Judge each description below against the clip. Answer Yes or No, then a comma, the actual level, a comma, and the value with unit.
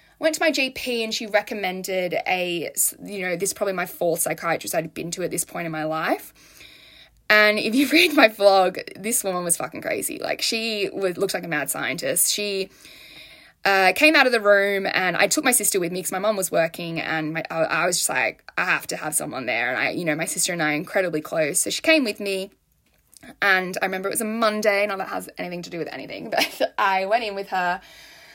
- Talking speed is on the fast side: Yes, fast, 240 wpm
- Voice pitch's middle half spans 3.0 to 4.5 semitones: Yes, average, 3.8 semitones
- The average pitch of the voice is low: No, high, 195 Hz